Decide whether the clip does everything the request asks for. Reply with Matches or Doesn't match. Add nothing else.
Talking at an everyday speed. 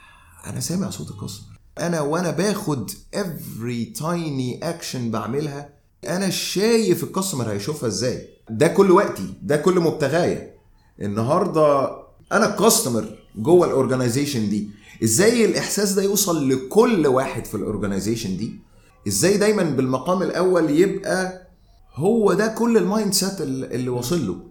Doesn't match